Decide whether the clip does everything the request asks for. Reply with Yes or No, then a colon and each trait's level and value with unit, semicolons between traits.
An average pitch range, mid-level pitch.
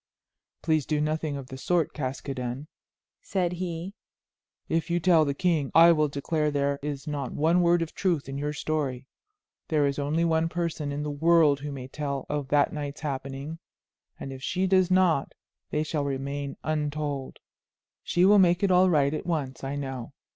Yes: average, 3.0 semitones; medium, 150 Hz